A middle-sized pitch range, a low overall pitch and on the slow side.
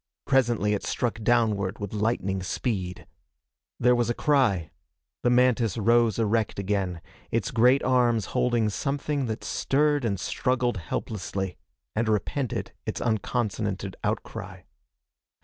Yes: average, 3.6 semitones; low, 115 Hz; slow, 120 wpm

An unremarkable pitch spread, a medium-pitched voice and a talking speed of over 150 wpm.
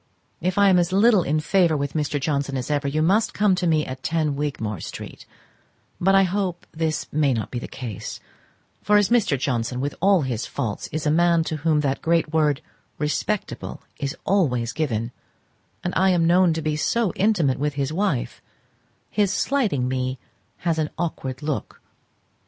Yes: average, 4.7 semitones; medium, 155 Hz; average, 180 wpm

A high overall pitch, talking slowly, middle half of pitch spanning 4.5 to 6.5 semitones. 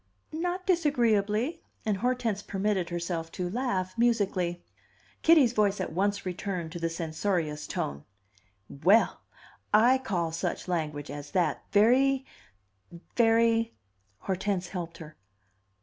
Yes: high, 195 Hz; slow, 120 wpm; average, 5.2 semitones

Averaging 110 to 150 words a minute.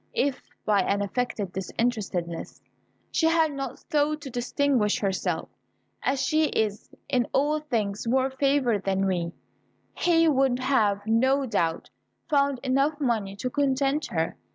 Yes: slow, 135 wpm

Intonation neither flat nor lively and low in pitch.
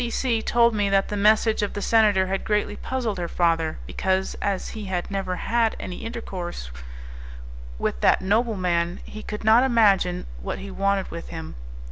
No: average, 3.4 semitones; high, 200 Hz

